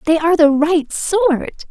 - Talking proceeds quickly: No, average, 175 wpm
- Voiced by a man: No, female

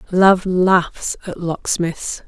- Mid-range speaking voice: Yes, medium, 180 Hz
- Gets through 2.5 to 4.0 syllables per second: Yes, 2.6 syllables/s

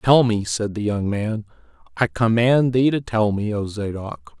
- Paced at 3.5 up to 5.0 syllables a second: Yes, 4.2 syllables/s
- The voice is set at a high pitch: No, low, 110 Hz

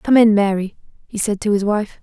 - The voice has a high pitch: Yes, high, 210 Hz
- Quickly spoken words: Yes, fast, 235 wpm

